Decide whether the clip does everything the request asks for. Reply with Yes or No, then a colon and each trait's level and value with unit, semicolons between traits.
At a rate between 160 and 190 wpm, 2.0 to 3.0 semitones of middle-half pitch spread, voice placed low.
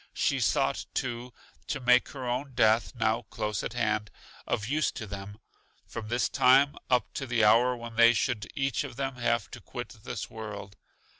Yes: average, 180 wpm; average, 2.7 semitones; low, 120 Hz